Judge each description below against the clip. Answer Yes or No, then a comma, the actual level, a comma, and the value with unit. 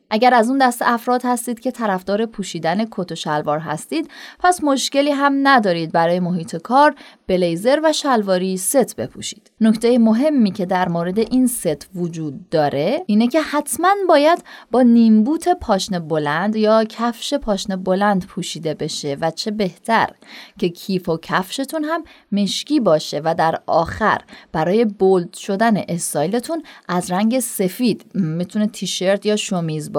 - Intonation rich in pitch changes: Yes, wide, 5.8 semitones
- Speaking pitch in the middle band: No, high, 210 Hz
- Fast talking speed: No, average, 145 wpm